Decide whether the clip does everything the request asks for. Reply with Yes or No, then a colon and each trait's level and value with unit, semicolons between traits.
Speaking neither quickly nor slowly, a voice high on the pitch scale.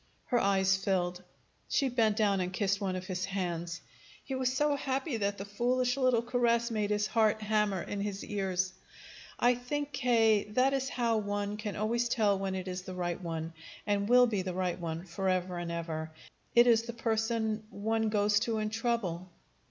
Yes: average, 190 wpm; high, 210 Hz